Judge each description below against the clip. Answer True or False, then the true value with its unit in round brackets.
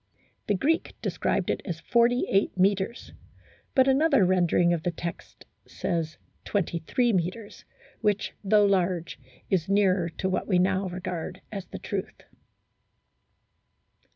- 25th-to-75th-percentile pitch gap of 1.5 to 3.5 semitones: True (2.9 semitones)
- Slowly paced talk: True (125 wpm)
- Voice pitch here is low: False (190 Hz)